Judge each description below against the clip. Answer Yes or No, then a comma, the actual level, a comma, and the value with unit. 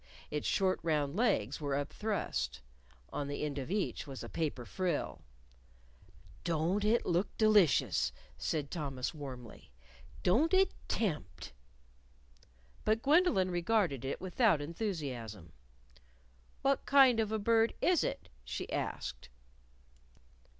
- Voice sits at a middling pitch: Yes, medium, 170 Hz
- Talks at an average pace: No, slow, 120 wpm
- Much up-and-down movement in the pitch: Yes, wide, 7.4 semitones